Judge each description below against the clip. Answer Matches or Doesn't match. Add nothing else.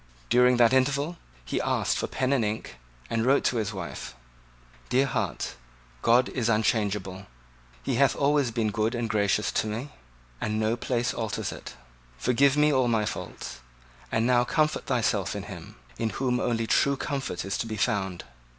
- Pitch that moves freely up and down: Doesn't match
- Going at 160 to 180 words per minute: Matches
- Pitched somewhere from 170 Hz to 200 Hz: Doesn't match